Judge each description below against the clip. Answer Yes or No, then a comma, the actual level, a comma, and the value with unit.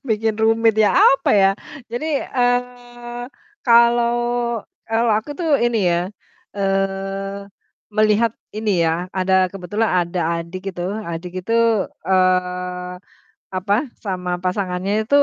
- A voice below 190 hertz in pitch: No, high, 200 Hz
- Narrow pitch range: No, average, 4.1 semitones